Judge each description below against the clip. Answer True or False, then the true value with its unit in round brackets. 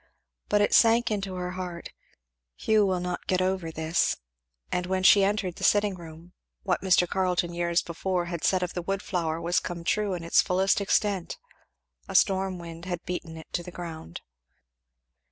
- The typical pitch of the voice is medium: True (180 Hz)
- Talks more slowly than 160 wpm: False (180 wpm)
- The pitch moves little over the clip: True (2.0 semitones)